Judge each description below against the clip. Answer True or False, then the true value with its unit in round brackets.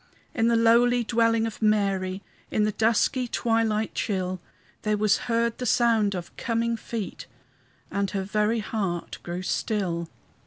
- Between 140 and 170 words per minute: True (145 wpm)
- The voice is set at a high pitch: True (215 Hz)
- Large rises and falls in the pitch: False (2.7 semitones)